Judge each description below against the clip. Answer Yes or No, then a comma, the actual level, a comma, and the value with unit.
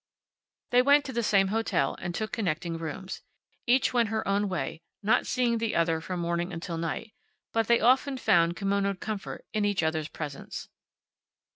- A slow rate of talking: No, average, 170 wpm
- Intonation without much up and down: No, average, 5.1 semitones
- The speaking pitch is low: No, high, 200 Hz